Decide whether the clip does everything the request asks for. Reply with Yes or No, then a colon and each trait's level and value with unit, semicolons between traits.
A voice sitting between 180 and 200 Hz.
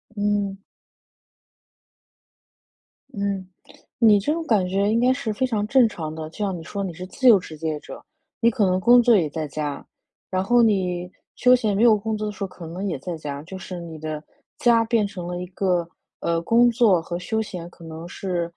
Yes: high, 195 Hz